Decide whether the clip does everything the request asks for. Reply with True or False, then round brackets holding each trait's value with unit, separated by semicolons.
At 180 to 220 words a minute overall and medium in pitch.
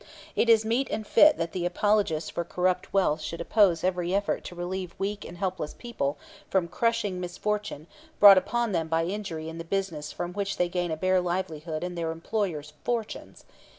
True (185 wpm; 180 Hz)